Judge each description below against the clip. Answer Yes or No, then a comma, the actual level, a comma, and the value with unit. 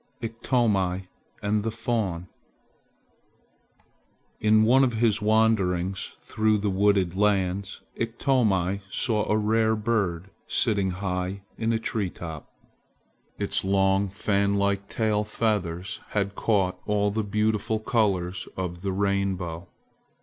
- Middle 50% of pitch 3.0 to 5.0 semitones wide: No, narrow, 2.5 semitones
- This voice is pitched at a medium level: No, low, 100 Hz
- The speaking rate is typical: No, slow, 115 wpm